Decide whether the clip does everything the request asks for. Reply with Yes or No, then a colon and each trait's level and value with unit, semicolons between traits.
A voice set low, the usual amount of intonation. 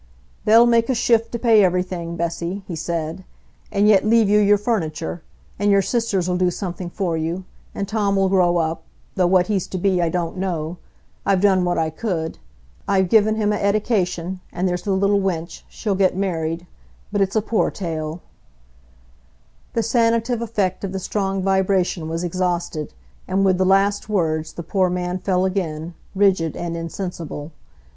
No: medium, 185 Hz; average, 3.0 semitones